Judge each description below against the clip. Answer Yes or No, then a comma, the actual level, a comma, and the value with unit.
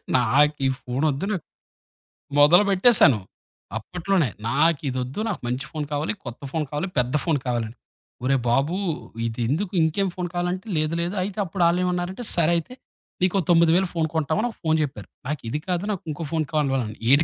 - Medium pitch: Yes, medium, 155 Hz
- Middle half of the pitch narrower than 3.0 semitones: No, average, 4.7 semitones